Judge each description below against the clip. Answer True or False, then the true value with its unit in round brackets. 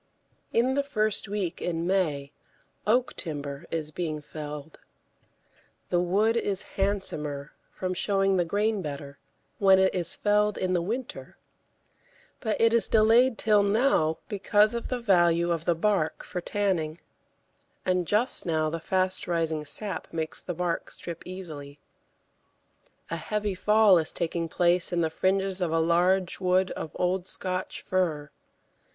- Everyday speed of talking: True (145 wpm)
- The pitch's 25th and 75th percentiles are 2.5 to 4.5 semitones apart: True (3.9 semitones)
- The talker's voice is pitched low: False (185 Hz)